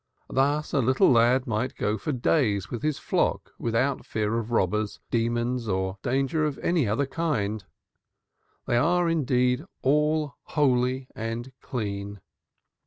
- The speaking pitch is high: No, low, 125 Hz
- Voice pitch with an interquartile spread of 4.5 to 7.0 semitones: No, average, 4.1 semitones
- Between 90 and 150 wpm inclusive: Yes, slow, 135 wpm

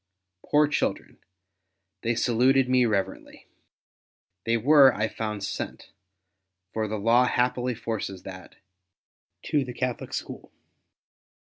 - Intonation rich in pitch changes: No, average, 3.2 semitones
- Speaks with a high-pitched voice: No, low, 115 Hz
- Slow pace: Yes, slow, 120 wpm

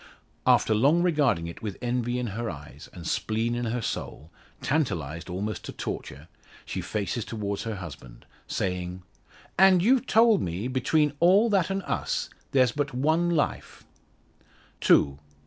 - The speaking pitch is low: Yes, low, 120 Hz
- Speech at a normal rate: Yes, average, 150 wpm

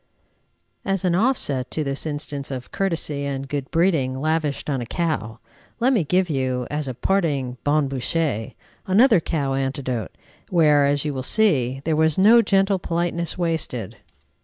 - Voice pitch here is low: No, medium, 150 Hz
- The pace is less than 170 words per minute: Yes, average, 160 wpm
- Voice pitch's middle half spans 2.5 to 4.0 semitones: No, average, 4.4 semitones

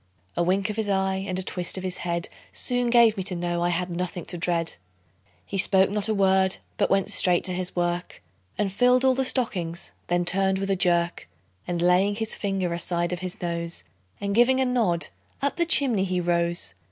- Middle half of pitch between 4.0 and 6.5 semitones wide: No, average, 2.7 semitones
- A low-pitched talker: No, medium, 185 Hz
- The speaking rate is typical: No, fast, 210 wpm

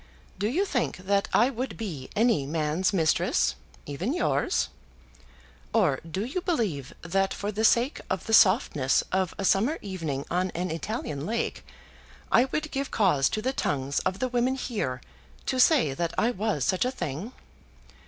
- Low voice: No, high, 200 Hz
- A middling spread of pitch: No, wide, 7.1 semitones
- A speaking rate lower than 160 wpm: No, average, 165 wpm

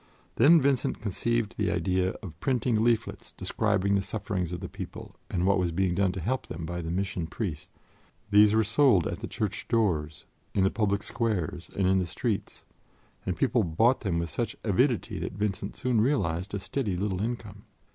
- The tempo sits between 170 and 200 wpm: Yes, average, 185 wpm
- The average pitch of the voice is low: Yes, low, 100 Hz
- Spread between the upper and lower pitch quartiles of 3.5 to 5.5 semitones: Yes, average, 4.0 semitones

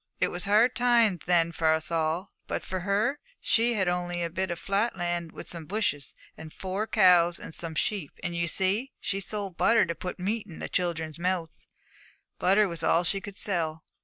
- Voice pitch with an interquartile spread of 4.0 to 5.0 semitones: No, average, 3.2 semitones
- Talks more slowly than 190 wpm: No, average, 200 wpm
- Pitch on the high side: No, medium, 180 Hz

